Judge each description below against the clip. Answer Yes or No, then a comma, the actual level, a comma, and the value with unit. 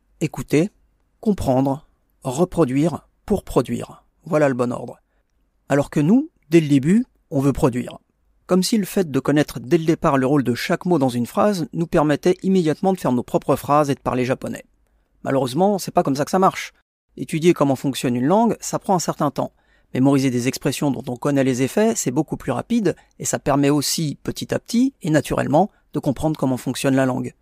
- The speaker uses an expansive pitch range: No, average, 4.6 semitones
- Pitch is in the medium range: Yes, medium, 145 Hz